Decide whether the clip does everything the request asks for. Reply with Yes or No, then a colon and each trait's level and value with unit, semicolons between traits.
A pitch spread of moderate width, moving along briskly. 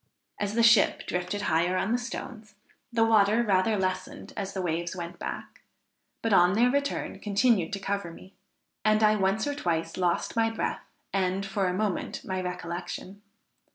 No: average, 3.2 semitones; average, 170 wpm